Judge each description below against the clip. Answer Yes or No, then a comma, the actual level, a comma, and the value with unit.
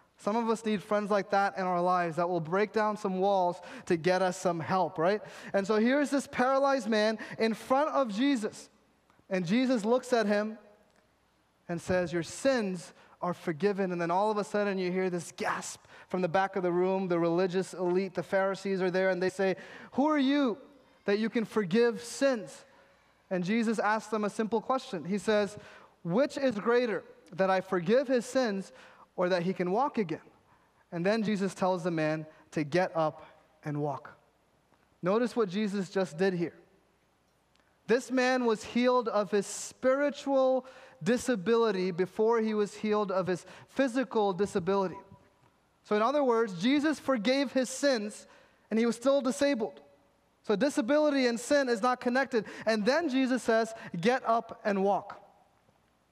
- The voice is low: No, high, 210 Hz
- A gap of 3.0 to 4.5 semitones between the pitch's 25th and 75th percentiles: No, average, 5.0 semitones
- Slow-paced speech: No, average, 170 wpm